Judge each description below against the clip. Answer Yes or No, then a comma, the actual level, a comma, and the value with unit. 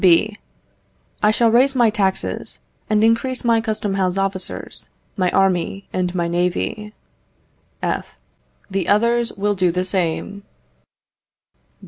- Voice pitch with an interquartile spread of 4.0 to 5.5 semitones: No, average, 3.3 semitones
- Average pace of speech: No, slow, 120 wpm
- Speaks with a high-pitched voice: Yes, high, 200 Hz